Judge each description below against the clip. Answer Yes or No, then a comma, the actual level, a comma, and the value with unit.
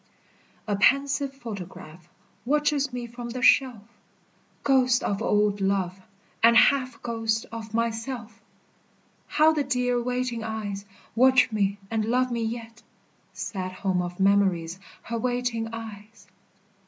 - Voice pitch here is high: Yes, high, 230 Hz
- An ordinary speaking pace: No, slow, 125 wpm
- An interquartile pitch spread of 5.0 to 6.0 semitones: No, average, 3.6 semitones